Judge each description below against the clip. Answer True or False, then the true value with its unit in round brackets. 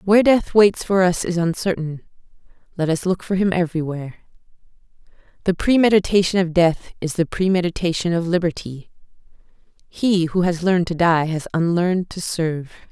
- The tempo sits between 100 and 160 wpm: True (150 wpm)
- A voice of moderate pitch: True (175 Hz)